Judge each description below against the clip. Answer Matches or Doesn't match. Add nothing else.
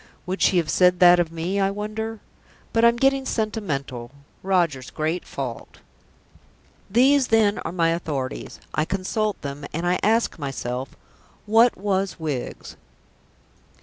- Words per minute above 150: Doesn't match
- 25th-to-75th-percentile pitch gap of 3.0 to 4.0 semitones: Doesn't match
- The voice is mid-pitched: Matches